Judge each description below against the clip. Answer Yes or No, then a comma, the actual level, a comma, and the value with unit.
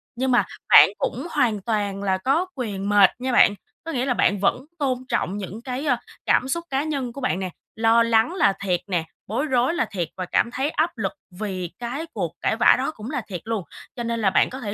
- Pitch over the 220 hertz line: Yes, high, 235 Hz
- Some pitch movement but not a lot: Yes, average, 4.7 semitones